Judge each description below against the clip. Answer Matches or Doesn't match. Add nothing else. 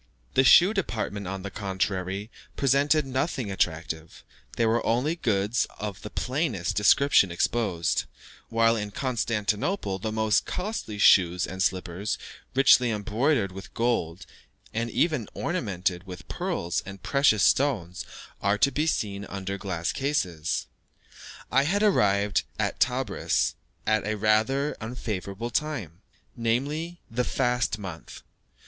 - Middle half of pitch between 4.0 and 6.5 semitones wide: Matches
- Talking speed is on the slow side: Matches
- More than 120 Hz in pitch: Doesn't match